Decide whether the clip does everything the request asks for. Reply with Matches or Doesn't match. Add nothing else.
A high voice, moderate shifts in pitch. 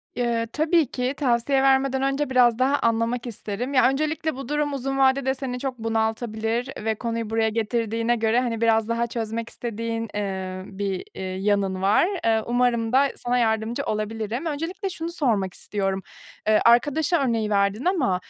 Matches